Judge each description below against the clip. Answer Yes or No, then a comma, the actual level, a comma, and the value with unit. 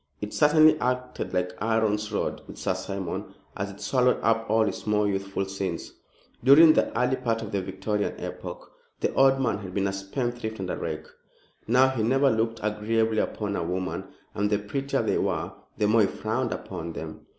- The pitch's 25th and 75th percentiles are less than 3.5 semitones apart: No, average, 4.1 semitones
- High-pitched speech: No, low, 105 Hz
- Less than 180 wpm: No, average, 190 wpm